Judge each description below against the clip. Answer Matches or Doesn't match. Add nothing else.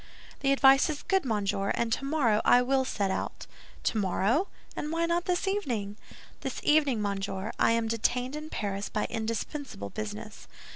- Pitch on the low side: Doesn't match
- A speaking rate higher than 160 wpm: Doesn't match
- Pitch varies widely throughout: Matches